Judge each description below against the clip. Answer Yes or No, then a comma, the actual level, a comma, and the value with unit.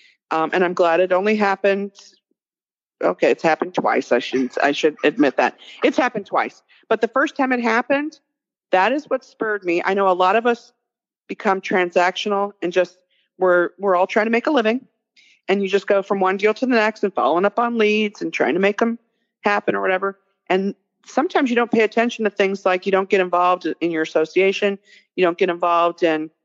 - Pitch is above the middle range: Yes, high, 200 Hz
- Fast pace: Yes, fast, 210 wpm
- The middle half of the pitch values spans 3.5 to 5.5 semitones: Yes, average, 4.1 semitones